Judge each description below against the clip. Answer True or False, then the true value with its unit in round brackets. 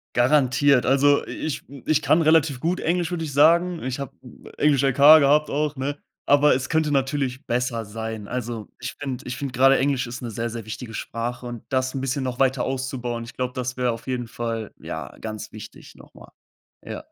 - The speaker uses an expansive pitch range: False (2.9 semitones)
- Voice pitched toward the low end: True (130 Hz)